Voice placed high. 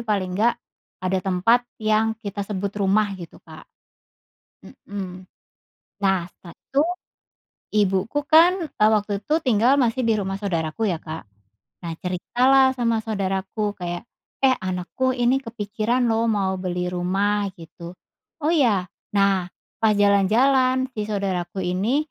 Yes: high, 205 Hz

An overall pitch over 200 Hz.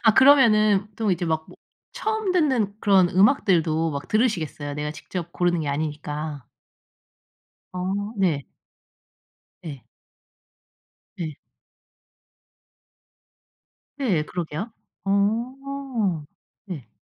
No: medium, 185 Hz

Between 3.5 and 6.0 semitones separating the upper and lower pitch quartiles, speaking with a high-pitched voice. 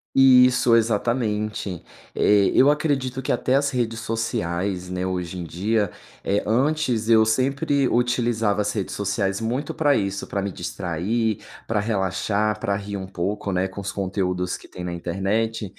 No: average, 3.9 semitones; low, 105 Hz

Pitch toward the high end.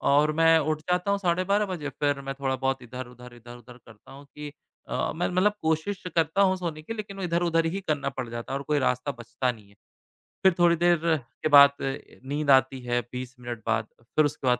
No: medium, 145 Hz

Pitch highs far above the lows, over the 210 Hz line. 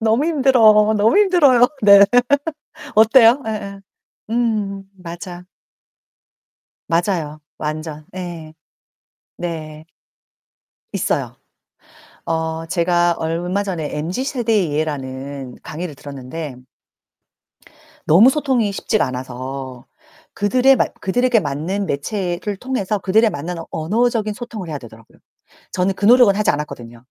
No: wide, 6.1 semitones; medium, 185 Hz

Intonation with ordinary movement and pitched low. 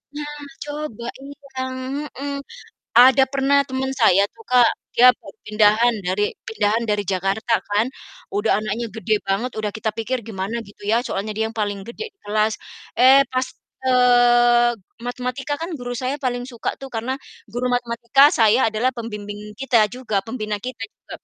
No: average, 3.4 semitones; high, 240 Hz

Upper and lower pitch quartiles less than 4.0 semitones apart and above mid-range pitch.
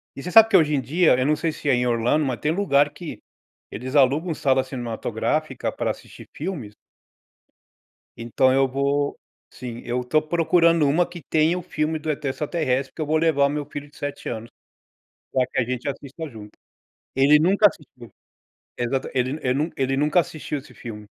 No: average, 3.5 semitones; medium, 145 Hz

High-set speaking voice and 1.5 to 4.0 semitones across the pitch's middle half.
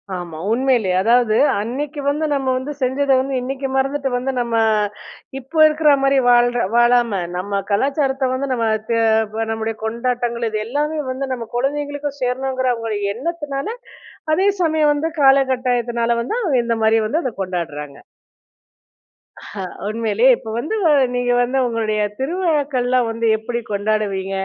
Yes: very high, 250 Hz; average, 3.3 semitones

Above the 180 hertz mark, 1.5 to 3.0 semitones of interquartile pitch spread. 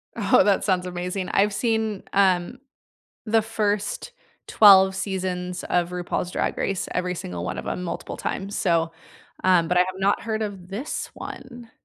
Yes: high, 190 Hz; narrow, 2.5 semitones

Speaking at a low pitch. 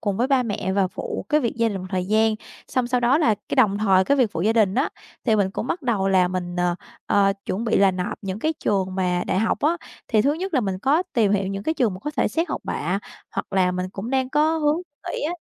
No: high, 210 Hz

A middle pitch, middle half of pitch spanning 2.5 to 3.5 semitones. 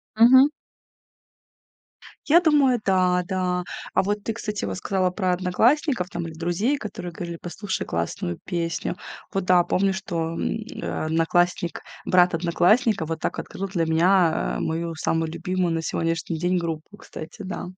Yes: medium, 180 Hz; average, 3.1 semitones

